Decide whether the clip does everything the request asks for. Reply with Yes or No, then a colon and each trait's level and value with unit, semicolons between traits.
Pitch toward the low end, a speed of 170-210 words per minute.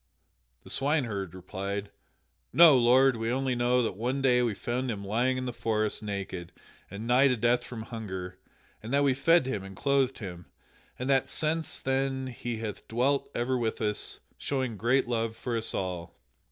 Yes: low, 120 Hz; average, 180 wpm